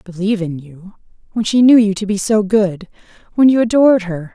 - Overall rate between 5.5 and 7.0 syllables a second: Yes, 5.6 syllables/s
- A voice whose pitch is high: Yes, high, 205 Hz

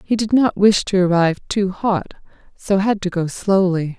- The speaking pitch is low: No, high, 190 Hz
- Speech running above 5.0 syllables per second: No, 4.6 syllables/s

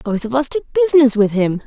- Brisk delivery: Yes, fast, 255 wpm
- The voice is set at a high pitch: Yes, very high, 255 Hz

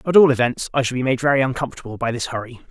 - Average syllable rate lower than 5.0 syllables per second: No, 7.8 syllables/s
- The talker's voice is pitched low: Yes, low, 130 Hz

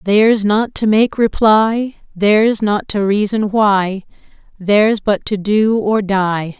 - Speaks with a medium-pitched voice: No, high, 210 Hz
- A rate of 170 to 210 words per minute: No, average, 145 wpm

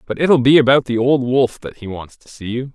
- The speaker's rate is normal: No, fast, 285 wpm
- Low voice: Yes, low, 125 Hz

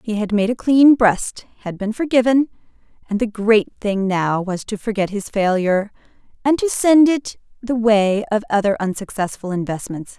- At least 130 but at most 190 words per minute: Yes, average, 170 wpm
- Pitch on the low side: No, high, 215 Hz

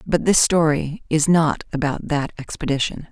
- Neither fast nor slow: Yes, average, 155 wpm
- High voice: No, medium, 155 Hz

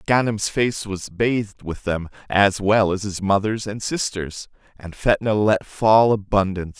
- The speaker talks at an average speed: Yes, average, 160 wpm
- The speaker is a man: Yes, male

